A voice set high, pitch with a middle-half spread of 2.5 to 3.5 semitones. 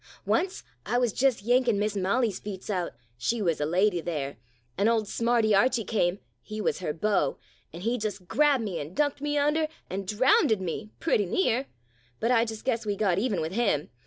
No: high, 215 Hz; average, 4.8 semitones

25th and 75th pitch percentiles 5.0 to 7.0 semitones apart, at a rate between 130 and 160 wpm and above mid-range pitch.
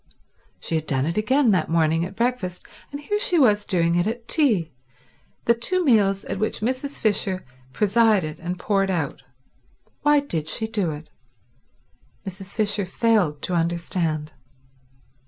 Yes: wide, 5.5 semitones; average, 150 wpm; high, 195 Hz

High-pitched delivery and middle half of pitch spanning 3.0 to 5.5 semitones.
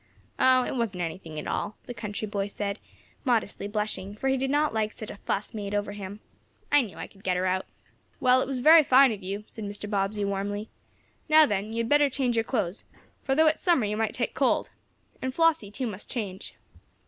Yes: high, 215 Hz; average, 4.4 semitones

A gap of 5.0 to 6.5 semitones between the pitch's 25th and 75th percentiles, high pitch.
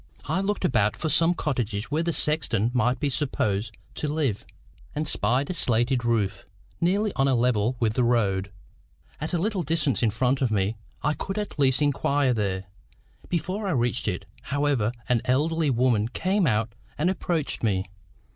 No: wide, 5.6 semitones; low, 130 Hz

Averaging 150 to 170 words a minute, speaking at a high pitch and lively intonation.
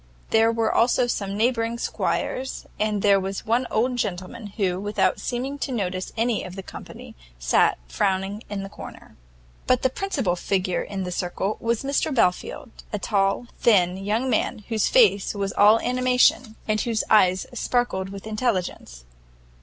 No: average, 160 wpm; high, 215 Hz; average, 3.9 semitones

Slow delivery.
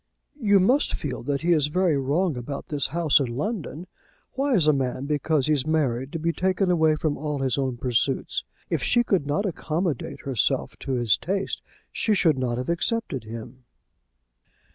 No: average, 180 wpm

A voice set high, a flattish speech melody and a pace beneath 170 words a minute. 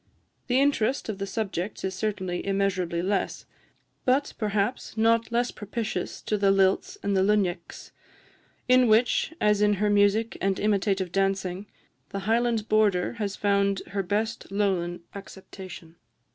Yes: high, 200 Hz; narrow, 2.2 semitones; average, 140 wpm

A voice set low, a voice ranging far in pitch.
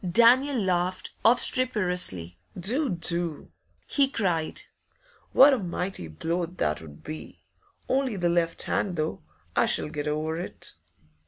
No: medium, 175 Hz; wide, 6.4 semitones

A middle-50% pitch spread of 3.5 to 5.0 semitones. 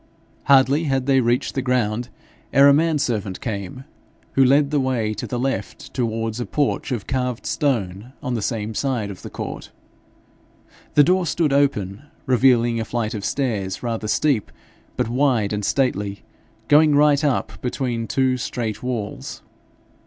Yes: average, 3.9 semitones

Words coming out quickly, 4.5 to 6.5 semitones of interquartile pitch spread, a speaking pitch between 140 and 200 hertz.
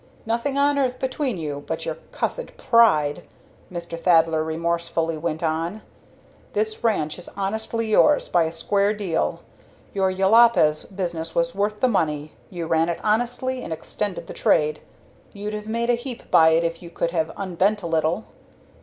No: average, 165 wpm; average, 5.2 semitones; medium, 185 Hz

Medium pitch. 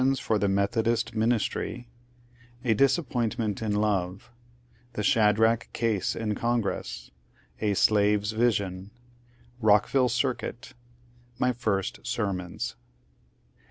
No: low, 110 Hz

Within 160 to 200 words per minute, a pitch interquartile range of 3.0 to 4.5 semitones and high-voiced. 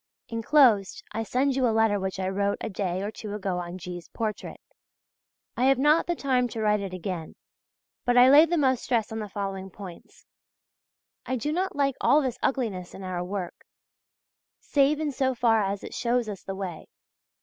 No: average, 195 wpm; average, 5.2 semitones; high, 220 Hz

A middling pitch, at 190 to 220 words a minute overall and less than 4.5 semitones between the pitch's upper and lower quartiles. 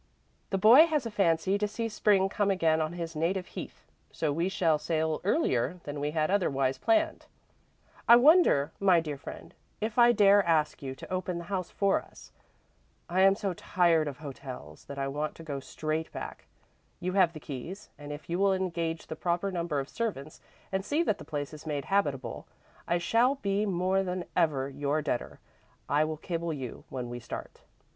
No: medium, 170 Hz; average, 195 wpm; average, 4.8 semitones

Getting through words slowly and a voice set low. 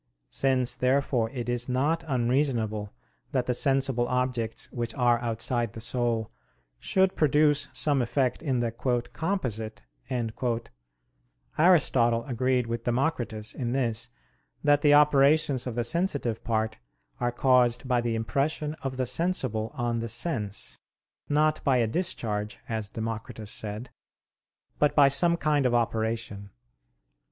Yes: slow, 130 wpm; low, 120 Hz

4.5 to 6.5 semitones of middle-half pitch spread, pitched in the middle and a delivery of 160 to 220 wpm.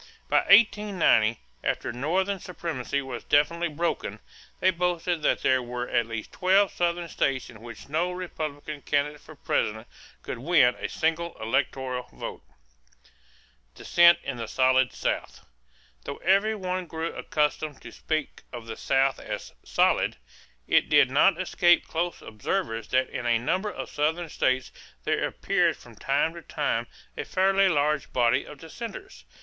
No: wide, 5.4 semitones; medium, 155 Hz; average, 150 wpm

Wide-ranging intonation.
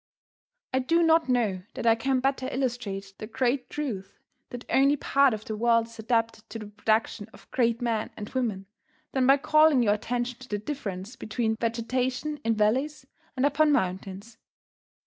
No: average, 3.5 semitones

